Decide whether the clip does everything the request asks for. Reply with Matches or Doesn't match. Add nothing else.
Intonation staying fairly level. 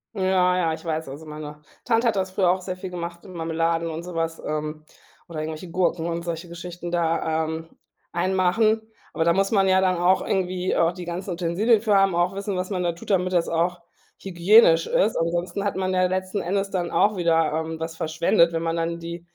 Matches